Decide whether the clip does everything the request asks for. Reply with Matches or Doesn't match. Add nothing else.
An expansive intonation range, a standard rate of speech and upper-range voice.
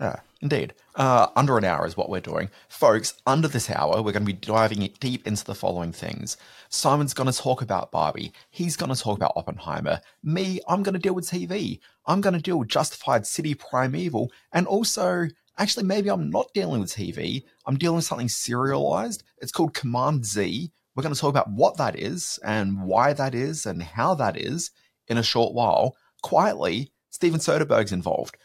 Doesn't match